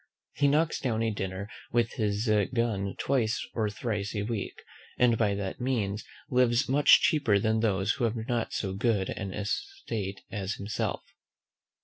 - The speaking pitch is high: No, low, 110 Hz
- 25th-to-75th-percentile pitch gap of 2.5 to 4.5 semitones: Yes, average, 3.0 semitones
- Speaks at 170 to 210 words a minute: No, average, 155 wpm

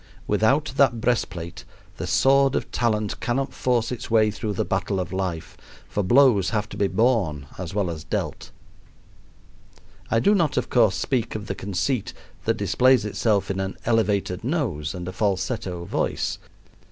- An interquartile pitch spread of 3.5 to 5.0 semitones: Yes, average, 4.6 semitones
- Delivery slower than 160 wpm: No, average, 165 wpm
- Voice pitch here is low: Yes, low, 105 Hz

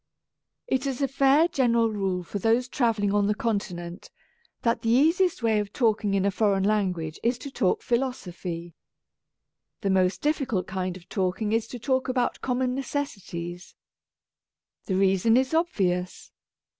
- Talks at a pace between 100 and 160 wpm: Yes, average, 155 wpm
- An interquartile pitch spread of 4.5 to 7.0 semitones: Yes, average, 5.1 semitones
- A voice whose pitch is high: Yes, high, 215 Hz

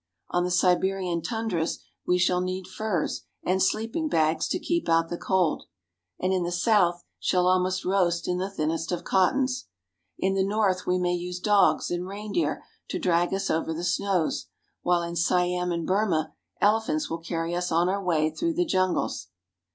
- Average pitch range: No, narrow, 2.1 semitones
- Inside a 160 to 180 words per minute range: Yes, average, 175 wpm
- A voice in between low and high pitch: Yes, medium, 180 Hz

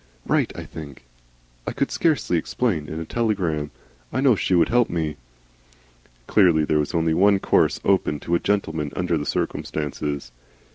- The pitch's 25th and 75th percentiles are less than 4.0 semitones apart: No, average, 4.6 semitones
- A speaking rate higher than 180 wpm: No, average, 160 wpm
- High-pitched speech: No, very low, 80 Hz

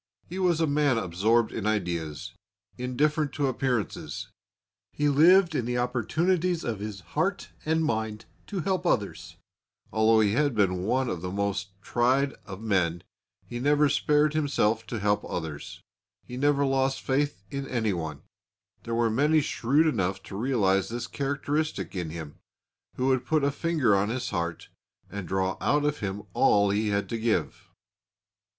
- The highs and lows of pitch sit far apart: Yes, wide, 6.5 semitones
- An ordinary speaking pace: Yes, average, 160 wpm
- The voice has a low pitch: Yes, low, 120 Hz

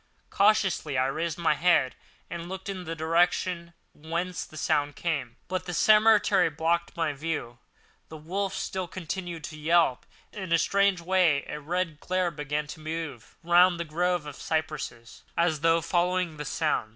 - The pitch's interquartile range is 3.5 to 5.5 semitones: No, average, 3.0 semitones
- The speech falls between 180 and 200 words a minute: No, average, 165 wpm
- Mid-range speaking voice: Yes, medium, 165 Hz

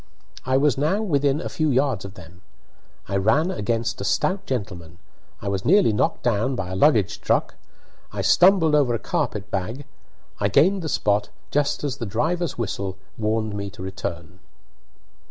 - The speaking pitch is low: Yes, low, 115 Hz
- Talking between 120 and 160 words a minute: No, average, 170 wpm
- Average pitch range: No, wide, 6.9 semitones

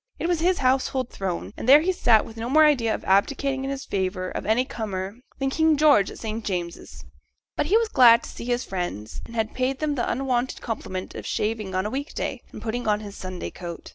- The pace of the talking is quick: Yes, fast, 230 wpm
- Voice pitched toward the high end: Yes, high, 235 Hz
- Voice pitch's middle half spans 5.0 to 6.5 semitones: Yes, wide, 5.4 semitones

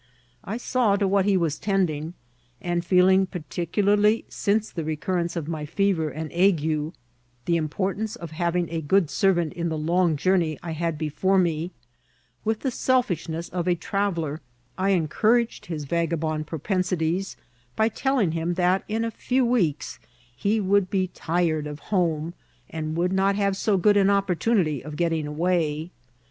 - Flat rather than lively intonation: No, average, 3.6 semitones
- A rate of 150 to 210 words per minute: Yes, average, 160 wpm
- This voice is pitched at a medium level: Yes, medium, 175 Hz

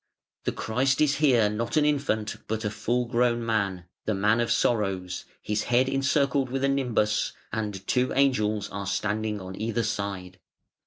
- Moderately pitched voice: No, low, 110 Hz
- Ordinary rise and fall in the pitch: Yes, average, 3.7 semitones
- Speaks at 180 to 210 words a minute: No, average, 165 wpm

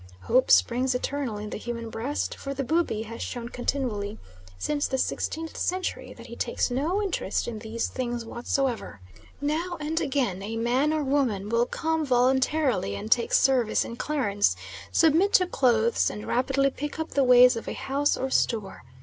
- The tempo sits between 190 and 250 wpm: No, average, 175 wpm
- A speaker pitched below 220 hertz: No, very high, 255 Hz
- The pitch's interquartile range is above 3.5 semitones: Yes, average, 4.0 semitones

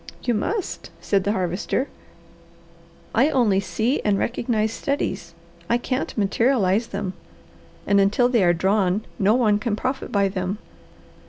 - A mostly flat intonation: No, average, 3.7 semitones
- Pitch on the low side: No, high, 210 Hz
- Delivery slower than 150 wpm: Yes, average, 140 wpm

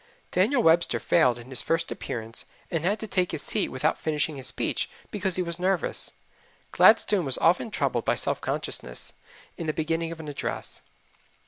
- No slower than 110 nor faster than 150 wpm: No, average, 180 wpm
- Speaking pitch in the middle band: Yes, medium, 165 Hz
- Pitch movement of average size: Yes, average, 4.5 semitones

